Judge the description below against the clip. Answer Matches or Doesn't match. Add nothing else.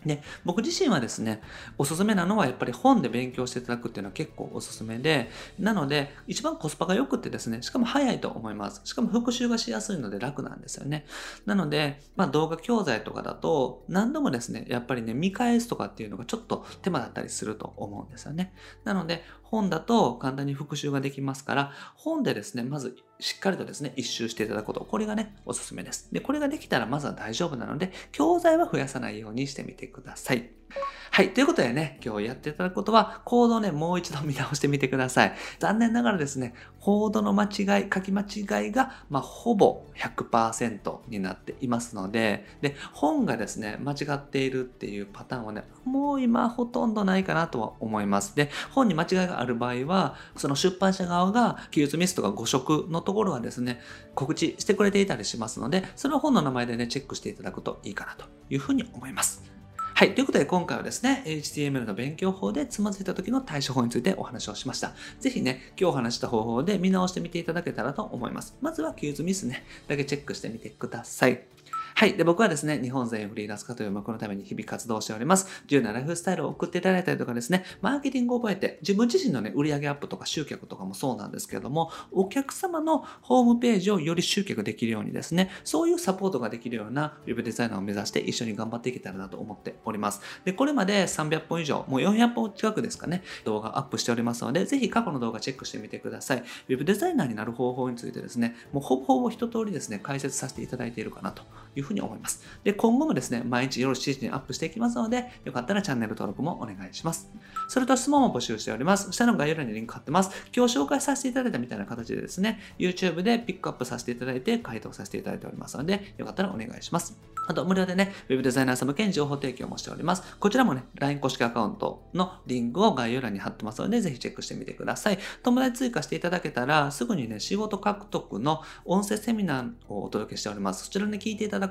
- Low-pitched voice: Doesn't match